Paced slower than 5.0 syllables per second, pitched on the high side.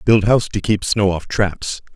No: 4.7 syllables/s; low, 100 Hz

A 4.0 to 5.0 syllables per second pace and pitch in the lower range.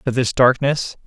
Yes: 4.4 syllables/s; low, 130 Hz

